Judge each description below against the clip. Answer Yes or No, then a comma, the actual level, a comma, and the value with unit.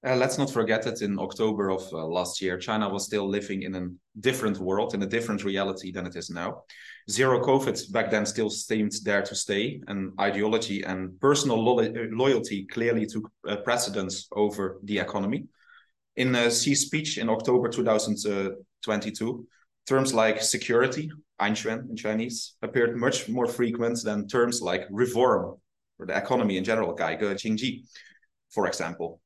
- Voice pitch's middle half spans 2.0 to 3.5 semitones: Yes, average, 3.2 semitones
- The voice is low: Yes, low, 110 Hz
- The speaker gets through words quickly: Yes, fast, 160 wpm